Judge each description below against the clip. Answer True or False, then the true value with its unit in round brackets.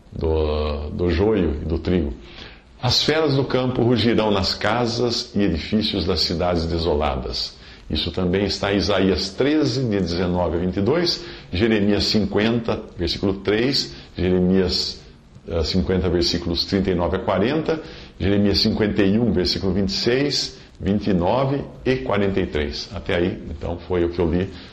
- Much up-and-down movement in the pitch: False (3.8 semitones)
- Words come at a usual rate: False (130 wpm)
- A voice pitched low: True (95 Hz)